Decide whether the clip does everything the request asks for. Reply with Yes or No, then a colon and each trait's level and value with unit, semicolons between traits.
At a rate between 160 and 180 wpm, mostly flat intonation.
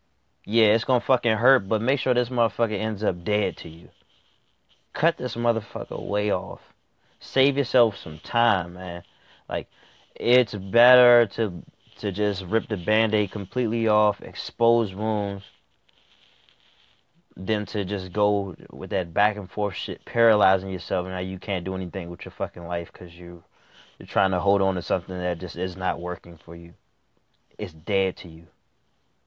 No: average, 165 wpm; average, 4.0 semitones